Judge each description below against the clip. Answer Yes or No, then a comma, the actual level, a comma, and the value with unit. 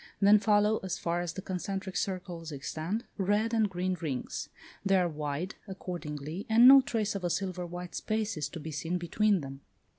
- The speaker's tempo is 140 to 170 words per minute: No, average, 185 wpm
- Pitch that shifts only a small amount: No, average, 3.8 semitones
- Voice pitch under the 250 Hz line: Yes, medium, 185 Hz